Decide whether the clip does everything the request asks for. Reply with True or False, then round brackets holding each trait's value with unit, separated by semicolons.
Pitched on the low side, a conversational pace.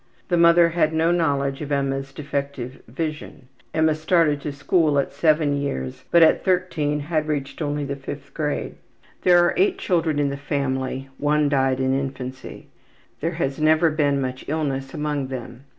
False (145 Hz; 170 wpm)